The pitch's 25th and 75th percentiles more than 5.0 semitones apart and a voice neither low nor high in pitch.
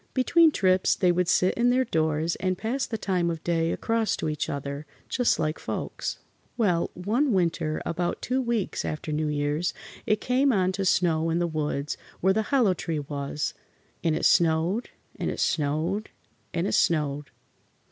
Yes: wide, 5.5 semitones; medium, 175 Hz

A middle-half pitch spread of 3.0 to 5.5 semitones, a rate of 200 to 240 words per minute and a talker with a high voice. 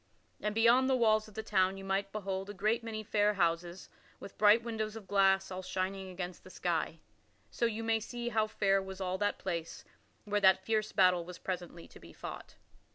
No: narrow, 2.5 semitones; fast, 205 wpm; high, 195 Hz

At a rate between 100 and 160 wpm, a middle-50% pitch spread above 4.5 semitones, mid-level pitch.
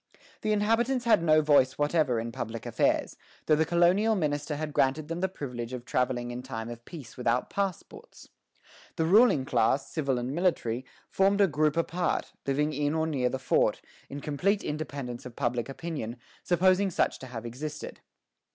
No: average, 170 wpm; average, 5.3 semitones; medium, 150 Hz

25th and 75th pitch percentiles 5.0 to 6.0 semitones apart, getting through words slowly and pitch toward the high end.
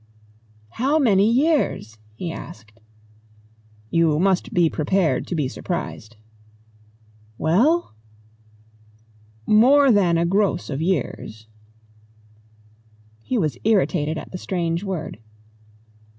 No: wide, 5.4 semitones; slow, 95 wpm; medium, 180 Hz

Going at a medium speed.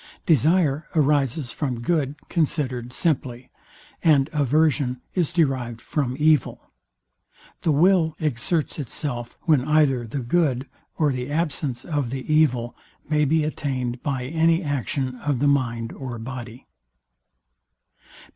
No: slow, 120 wpm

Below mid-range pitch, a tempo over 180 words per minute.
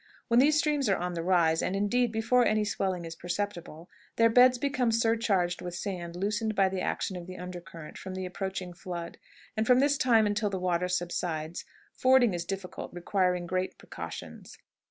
No: high, 190 Hz; average, 190 wpm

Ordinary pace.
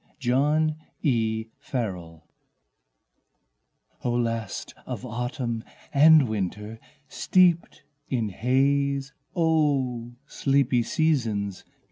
No: slow, 75 wpm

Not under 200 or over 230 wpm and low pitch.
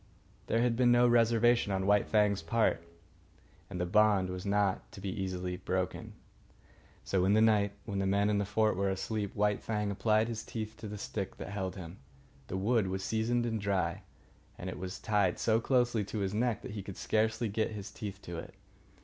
Yes: fast, 205 wpm; low, 105 Hz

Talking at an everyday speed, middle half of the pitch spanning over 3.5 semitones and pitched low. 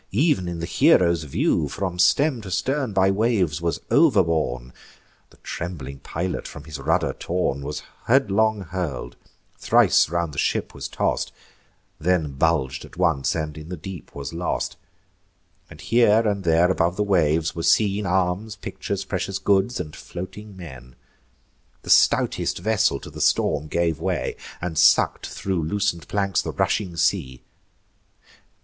Yes: average, 150 wpm; average, 4.0 semitones; very low, 90 Hz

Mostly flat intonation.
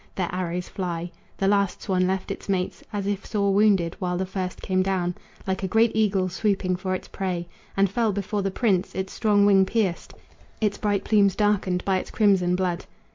Yes: narrow, 1.8 semitones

